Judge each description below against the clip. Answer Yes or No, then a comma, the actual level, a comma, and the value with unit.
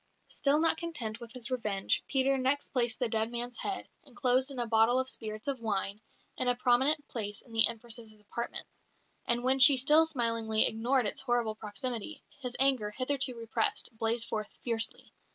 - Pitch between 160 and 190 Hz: No, high, 240 Hz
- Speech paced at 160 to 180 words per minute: Yes, average, 175 wpm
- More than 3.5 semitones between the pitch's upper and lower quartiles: No, average, 3.0 semitones